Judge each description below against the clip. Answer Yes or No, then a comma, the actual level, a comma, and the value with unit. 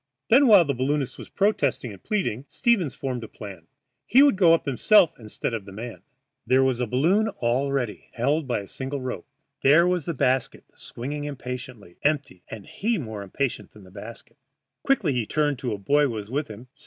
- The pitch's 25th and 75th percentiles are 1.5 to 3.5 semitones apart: No, average, 5.1 semitones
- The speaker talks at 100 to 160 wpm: No, average, 200 wpm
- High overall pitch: No, low, 130 Hz